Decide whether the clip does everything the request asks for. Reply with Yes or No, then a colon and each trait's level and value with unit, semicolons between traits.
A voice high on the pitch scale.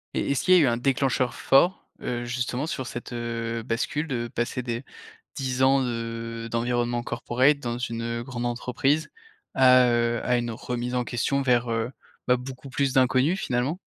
No: low, 125 Hz